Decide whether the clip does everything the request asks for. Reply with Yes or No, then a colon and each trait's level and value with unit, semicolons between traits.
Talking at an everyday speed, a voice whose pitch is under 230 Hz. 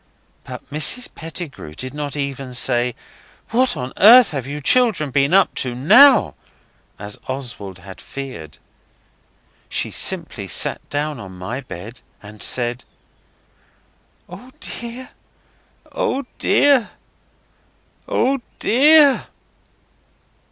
No: slow, 105 wpm; medium, 140 Hz